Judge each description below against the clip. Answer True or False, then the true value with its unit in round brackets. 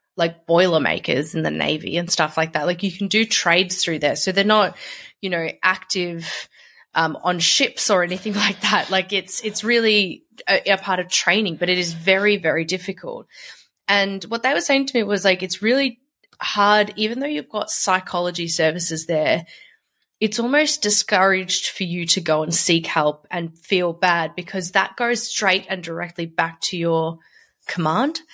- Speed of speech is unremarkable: True (180 wpm)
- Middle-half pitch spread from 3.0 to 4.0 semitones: True (3.7 semitones)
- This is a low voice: False (185 Hz)